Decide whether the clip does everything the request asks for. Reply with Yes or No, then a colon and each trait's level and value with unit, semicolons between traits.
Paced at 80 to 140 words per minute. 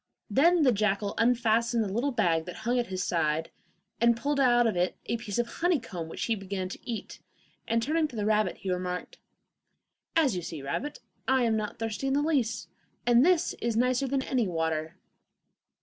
No: average, 195 wpm